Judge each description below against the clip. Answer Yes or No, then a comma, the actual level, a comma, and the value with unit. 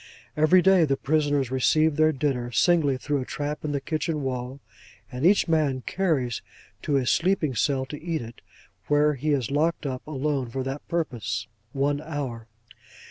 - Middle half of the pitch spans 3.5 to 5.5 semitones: No, average, 3.0 semitones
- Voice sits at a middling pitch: Yes, medium, 145 Hz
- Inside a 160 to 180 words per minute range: Yes, average, 175 wpm